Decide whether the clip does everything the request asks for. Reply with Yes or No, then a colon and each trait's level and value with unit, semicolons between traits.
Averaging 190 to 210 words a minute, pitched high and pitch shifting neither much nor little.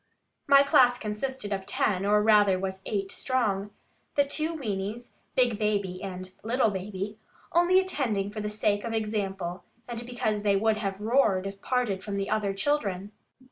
No: average, 165 wpm; high, 210 Hz; average, 3.6 semitones